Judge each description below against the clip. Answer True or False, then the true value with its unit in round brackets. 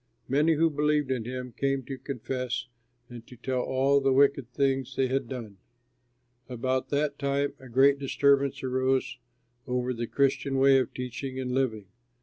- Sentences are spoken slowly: False (160 wpm)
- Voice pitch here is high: False (130 Hz)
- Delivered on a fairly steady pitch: True (1.6 semitones)